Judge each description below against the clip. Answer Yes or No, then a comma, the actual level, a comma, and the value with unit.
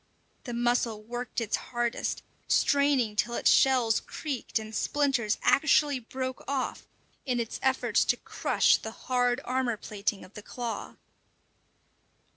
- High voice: Yes, high, 245 Hz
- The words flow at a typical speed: No, slow, 130 wpm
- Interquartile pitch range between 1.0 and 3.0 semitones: Yes, narrow, 2.5 semitones